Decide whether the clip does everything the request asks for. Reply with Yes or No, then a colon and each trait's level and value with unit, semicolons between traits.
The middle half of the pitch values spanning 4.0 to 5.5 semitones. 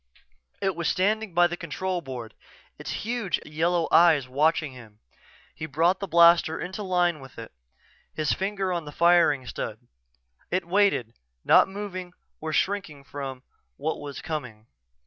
Yes: average, 4.3 semitones